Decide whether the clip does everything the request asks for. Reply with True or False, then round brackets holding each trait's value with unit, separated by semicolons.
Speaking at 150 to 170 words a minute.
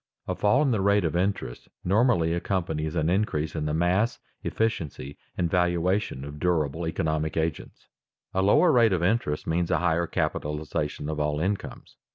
True (165 wpm)